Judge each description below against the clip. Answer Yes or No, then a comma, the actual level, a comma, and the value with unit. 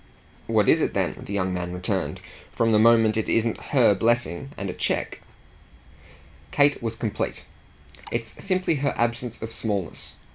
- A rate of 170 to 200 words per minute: No, average, 155 wpm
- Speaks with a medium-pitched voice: No, low, 115 Hz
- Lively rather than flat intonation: No, average, 2.9 semitones